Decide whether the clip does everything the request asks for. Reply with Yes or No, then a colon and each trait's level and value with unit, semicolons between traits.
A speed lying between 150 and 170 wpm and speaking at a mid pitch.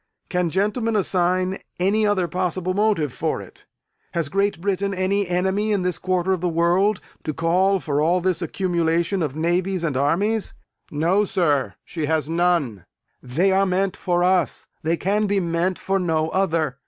Yes: average, 165 wpm; medium, 180 Hz